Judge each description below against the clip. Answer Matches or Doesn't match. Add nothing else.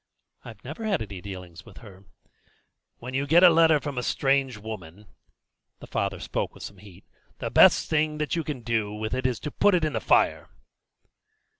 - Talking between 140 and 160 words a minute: Doesn't match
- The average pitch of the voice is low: Matches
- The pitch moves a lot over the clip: Matches